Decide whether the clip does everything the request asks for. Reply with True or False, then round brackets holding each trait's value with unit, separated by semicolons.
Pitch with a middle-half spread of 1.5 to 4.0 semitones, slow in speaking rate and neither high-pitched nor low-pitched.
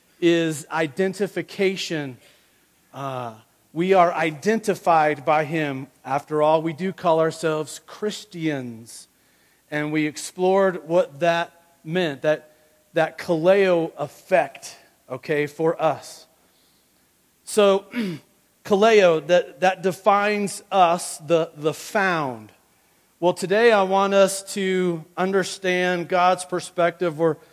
True (3.4 semitones; 100 wpm; 170 Hz)